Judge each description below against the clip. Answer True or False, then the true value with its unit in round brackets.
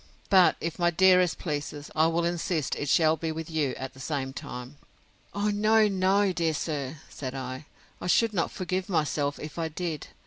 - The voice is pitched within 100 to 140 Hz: False (160 Hz)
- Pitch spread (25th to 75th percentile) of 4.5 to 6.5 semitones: False (3.9 semitones)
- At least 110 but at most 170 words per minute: False (185 wpm)